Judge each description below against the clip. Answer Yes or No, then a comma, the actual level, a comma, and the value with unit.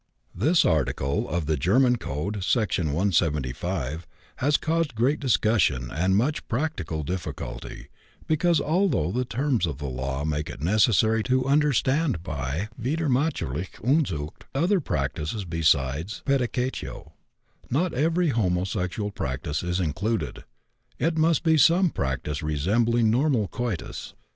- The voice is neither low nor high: No, low, 105 Hz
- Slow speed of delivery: Yes, slow, 120 wpm